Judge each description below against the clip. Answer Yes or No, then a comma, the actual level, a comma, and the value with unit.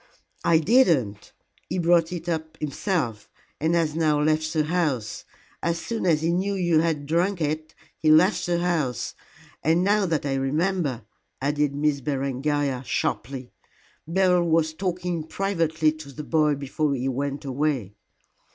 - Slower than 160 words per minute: Yes, average, 150 wpm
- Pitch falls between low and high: Yes, medium, 155 Hz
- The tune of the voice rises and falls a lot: No, average, 3.3 semitones